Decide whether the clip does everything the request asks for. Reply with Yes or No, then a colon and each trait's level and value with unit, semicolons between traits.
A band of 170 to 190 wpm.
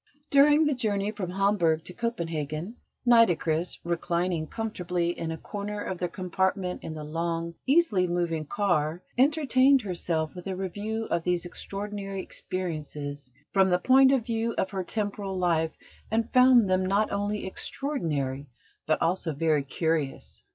No: average, 145 wpm